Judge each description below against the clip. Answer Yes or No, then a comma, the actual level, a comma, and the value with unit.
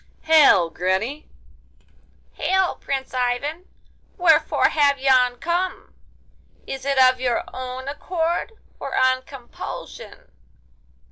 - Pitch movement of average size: Yes, average, 3.9 semitones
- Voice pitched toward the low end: No, very high, 275 Hz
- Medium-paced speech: No, slow, 95 wpm